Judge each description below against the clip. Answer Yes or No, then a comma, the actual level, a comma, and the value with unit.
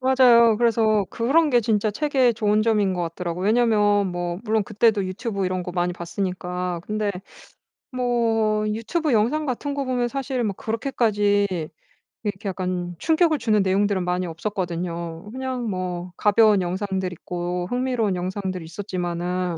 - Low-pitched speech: No, high, 205 Hz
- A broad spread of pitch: No, average, 4.3 semitones